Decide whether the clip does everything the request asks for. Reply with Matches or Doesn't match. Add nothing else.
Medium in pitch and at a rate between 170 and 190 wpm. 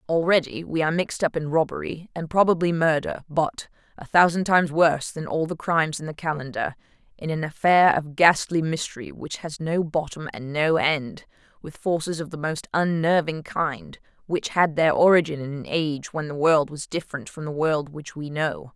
Matches